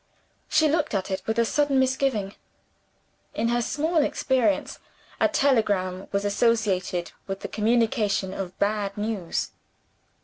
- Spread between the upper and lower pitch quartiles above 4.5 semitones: Yes, average, 4.9 semitones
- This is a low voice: No, high, 215 Hz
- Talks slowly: Yes, slow, 130 wpm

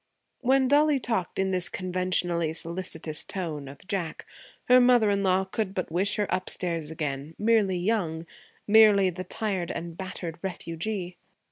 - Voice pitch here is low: No, medium, 185 Hz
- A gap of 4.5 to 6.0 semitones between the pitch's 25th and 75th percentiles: No, average, 3.7 semitones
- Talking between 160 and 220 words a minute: No, average, 145 wpm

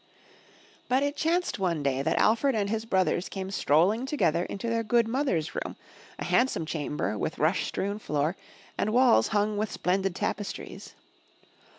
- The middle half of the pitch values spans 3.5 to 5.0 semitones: No, wide, 5.4 semitones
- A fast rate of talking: No, average, 160 wpm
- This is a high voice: Yes, high, 200 Hz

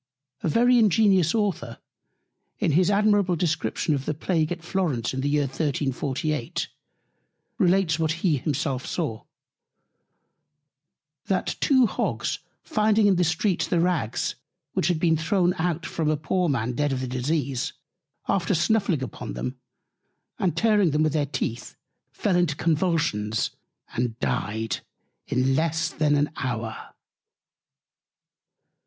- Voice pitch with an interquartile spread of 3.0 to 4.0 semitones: No, average, 5.2 semitones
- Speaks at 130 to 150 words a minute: Yes, slow, 135 wpm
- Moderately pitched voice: Yes, medium, 160 Hz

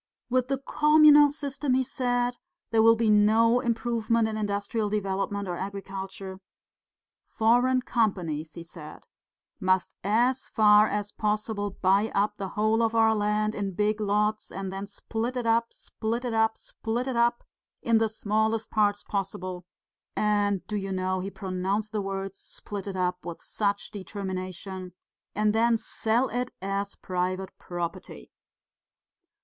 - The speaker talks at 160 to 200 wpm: No, average, 145 wpm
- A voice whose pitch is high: Yes, high, 210 Hz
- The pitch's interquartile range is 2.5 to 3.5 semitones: Yes, average, 2.8 semitones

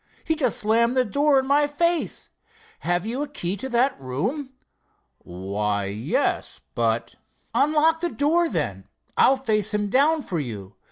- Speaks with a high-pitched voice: Yes, high, 235 Hz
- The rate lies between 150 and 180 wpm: Yes, average, 155 wpm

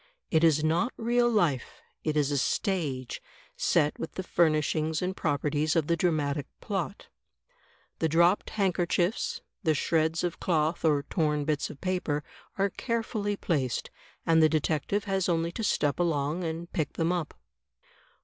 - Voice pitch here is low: No, medium, 165 Hz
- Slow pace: No, average, 155 wpm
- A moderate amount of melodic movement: Yes, average, 3.2 semitones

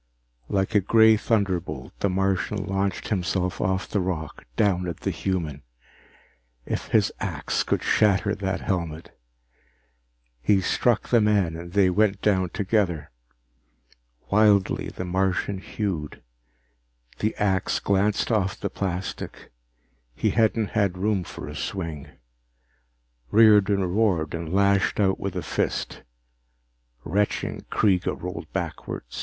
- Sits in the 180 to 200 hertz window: No, very low, 95 Hz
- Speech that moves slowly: Yes, slow, 125 wpm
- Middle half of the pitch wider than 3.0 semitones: No, narrow, 2.4 semitones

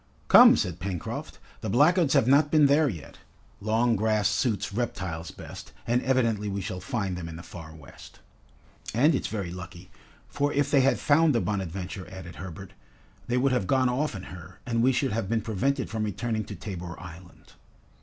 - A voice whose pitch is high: No, low, 105 Hz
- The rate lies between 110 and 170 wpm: No, average, 185 wpm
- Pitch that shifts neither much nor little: No, wide, 5.9 semitones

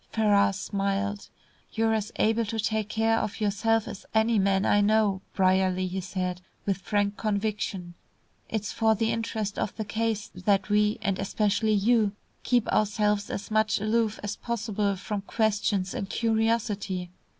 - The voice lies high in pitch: Yes, high, 210 Hz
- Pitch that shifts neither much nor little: No, narrow, 1.9 semitones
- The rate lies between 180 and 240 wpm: No, average, 150 wpm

